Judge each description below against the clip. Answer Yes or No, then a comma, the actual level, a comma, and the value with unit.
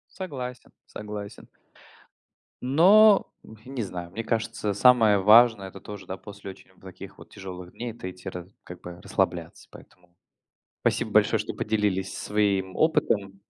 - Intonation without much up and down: No, average, 3.9 semitones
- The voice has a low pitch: Yes, low, 105 Hz